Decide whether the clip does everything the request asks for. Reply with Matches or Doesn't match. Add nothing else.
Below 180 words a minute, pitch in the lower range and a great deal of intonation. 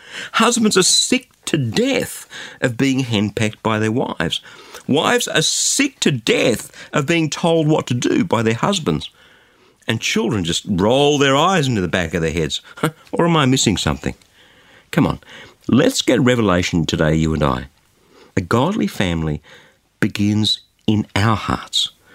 Matches